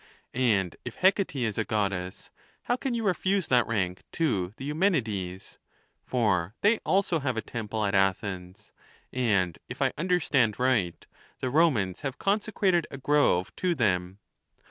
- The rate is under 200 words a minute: Yes, average, 150 wpm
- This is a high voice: No, low, 120 Hz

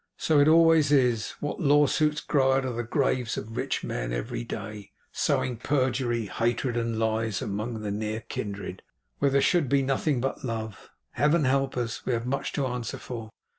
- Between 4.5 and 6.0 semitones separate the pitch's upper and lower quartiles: No, average, 3.7 semitones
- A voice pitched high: No, low, 125 Hz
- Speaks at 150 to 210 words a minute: Yes, average, 175 wpm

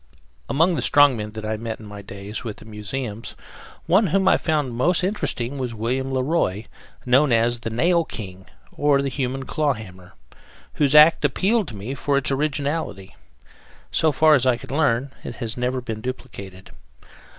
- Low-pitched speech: Yes, low, 130 Hz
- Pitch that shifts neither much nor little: Yes, average, 4.9 semitones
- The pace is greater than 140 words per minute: Yes, average, 175 wpm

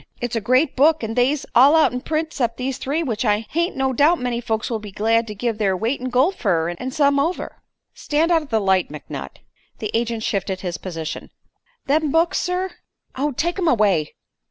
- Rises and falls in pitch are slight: No, wide, 5.5 semitones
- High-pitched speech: Yes, very high, 250 Hz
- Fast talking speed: Yes, fast, 210 wpm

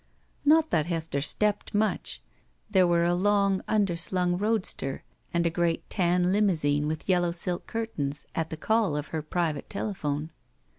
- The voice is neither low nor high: Yes, medium, 175 Hz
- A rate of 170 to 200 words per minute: No, average, 150 wpm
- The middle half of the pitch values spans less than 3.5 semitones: No, average, 4.1 semitones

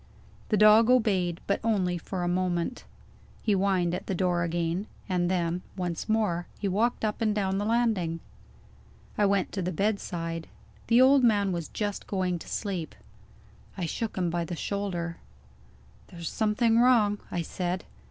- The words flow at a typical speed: Yes, average, 160 wpm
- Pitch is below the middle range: No, high, 190 Hz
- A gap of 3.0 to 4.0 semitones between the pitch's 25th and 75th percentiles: Yes, average, 3.4 semitones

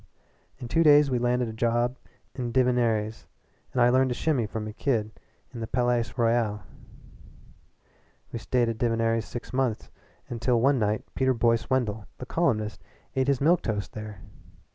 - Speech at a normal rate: Yes, average, 165 wpm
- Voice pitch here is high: No, low, 120 Hz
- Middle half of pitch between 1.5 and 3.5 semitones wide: Yes, narrow, 2.4 semitones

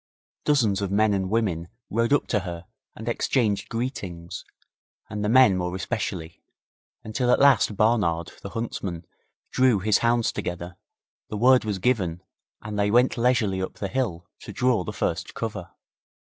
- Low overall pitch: Yes, low, 105 Hz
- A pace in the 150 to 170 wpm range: Yes, average, 155 wpm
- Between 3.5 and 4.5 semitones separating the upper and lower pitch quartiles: Yes, average, 4.2 semitones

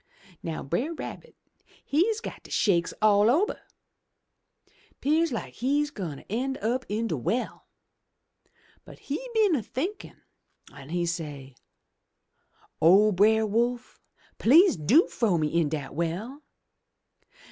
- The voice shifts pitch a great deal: Yes, wide, 8.7 semitones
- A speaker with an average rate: No, slow, 125 wpm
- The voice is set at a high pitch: Yes, high, 220 Hz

